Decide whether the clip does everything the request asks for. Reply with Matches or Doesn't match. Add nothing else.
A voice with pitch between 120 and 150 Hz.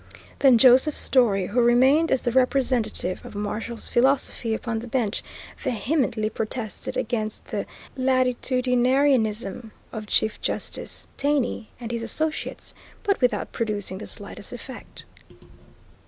Doesn't match